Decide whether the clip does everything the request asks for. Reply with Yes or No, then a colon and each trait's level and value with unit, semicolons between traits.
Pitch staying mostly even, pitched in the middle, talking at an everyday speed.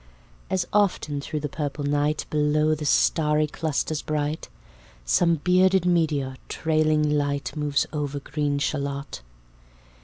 No: narrow, 1.5 semitones; medium, 150 Hz; slow, 120 wpm